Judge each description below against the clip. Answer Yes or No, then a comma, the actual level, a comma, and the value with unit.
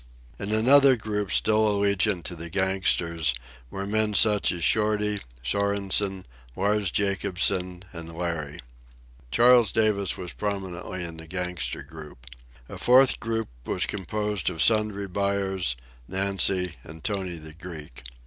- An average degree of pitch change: Yes, average, 3.4 semitones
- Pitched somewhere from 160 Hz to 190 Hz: No, very low, 95 Hz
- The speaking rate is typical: No, slow, 130 wpm